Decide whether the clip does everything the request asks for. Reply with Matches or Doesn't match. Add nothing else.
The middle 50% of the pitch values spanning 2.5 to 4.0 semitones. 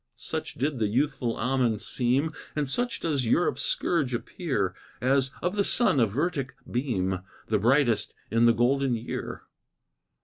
Doesn't match